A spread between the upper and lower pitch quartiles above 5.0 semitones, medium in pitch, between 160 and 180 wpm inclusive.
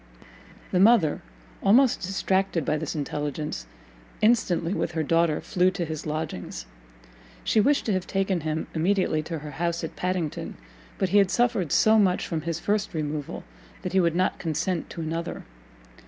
No: average, 3.6 semitones; medium, 170 Hz; average, 165 wpm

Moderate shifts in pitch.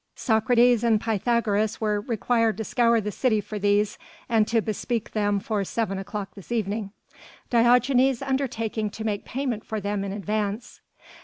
No: narrow, 2.3 semitones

